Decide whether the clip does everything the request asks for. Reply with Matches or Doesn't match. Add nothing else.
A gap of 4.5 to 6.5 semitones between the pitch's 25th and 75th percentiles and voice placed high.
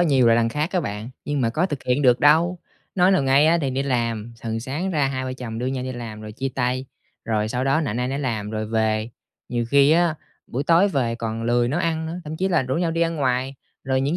Doesn't match